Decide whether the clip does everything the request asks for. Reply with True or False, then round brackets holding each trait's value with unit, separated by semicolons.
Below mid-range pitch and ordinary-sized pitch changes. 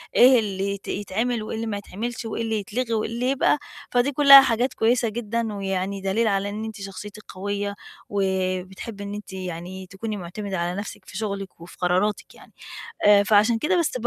False (205 Hz; 3.0 semitones)